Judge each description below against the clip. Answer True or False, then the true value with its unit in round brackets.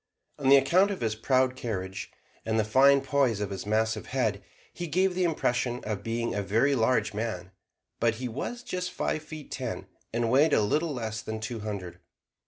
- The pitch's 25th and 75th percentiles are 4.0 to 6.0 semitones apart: True (4.4 semitones)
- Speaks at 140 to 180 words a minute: False (190 wpm)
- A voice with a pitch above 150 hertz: False (120 Hz)